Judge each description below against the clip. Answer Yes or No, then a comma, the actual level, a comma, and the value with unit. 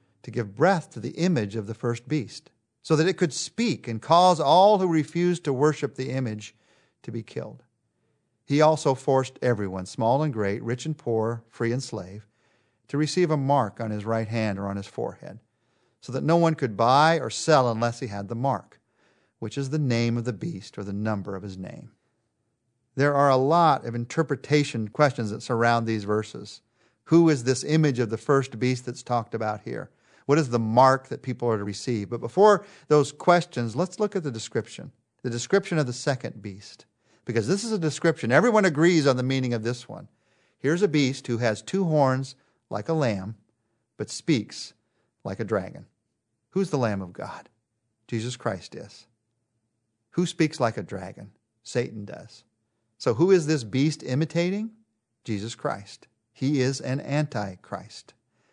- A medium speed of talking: Yes, average, 185 wpm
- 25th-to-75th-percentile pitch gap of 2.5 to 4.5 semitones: No, average, 5.1 semitones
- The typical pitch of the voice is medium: No, low, 125 Hz